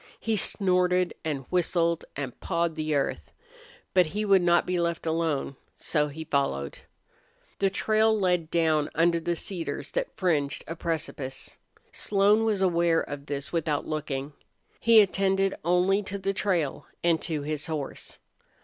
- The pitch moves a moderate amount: Yes, average, 3.8 semitones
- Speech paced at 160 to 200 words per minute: No, average, 145 wpm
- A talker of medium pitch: Yes, medium, 170 Hz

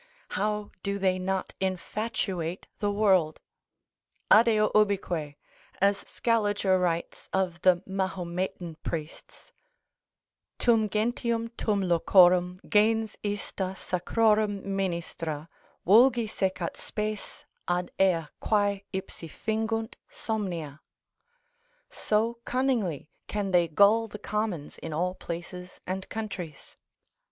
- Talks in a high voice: Yes, high, 195 Hz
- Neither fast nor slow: No, slow, 100 wpm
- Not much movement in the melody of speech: No, average, 3.2 semitones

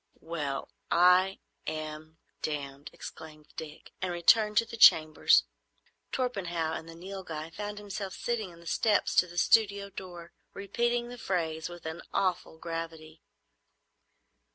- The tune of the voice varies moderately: Yes, average, 3.9 semitones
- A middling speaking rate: No, slow, 120 wpm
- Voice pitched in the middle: Yes, medium, 175 Hz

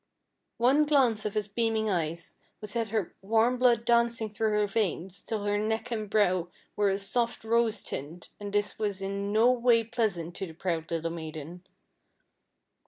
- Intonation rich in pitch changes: No, average, 3.2 semitones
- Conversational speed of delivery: Yes, average, 170 wpm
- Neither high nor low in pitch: No, high, 210 Hz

